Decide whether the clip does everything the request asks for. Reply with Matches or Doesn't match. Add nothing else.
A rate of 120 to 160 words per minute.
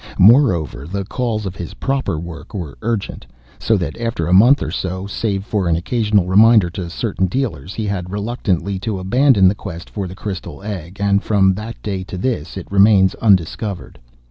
Doesn't match